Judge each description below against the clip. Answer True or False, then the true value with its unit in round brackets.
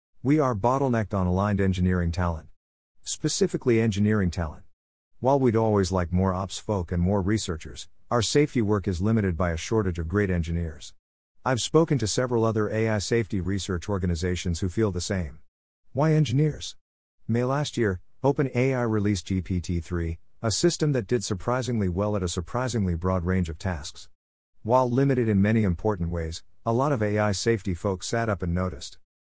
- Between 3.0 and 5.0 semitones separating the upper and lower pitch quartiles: True (4.7 semitones)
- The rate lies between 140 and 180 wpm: True (165 wpm)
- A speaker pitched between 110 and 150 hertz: False (100 Hz)